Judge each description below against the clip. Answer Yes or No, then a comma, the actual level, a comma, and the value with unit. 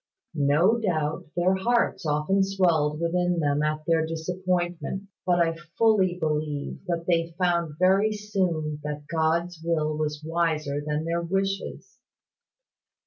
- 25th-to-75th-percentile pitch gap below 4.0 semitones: Yes, average, 3.2 semitones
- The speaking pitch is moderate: Yes, medium, 170 Hz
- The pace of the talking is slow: Yes, slow, 130 wpm